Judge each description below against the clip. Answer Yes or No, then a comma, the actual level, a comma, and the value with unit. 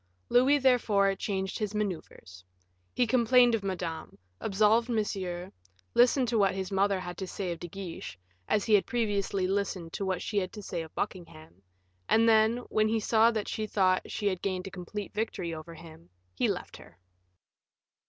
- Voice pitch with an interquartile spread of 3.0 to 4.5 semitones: Yes, average, 3.3 semitones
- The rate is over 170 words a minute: Yes, average, 180 wpm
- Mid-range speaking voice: No, high, 200 Hz